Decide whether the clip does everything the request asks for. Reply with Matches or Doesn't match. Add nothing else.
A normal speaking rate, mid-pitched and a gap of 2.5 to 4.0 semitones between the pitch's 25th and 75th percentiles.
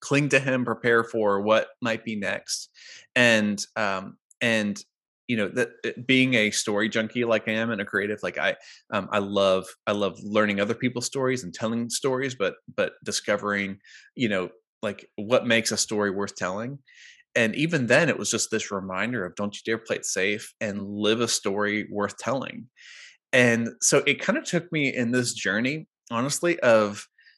Doesn't match